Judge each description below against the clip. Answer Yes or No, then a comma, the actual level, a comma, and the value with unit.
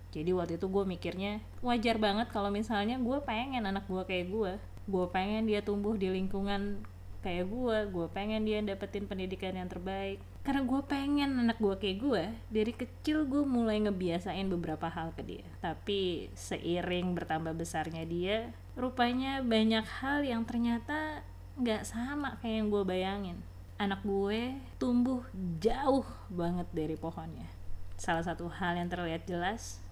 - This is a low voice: No, high, 195 Hz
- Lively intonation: No, average, 5.0 semitones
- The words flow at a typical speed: No, fast, 150 wpm